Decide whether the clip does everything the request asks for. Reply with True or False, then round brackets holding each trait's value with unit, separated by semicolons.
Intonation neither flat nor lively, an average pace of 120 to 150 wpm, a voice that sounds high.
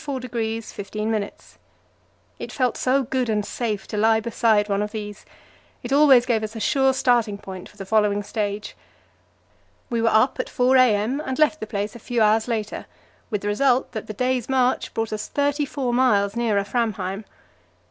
False (3.3 semitones; 175 wpm; 225 Hz)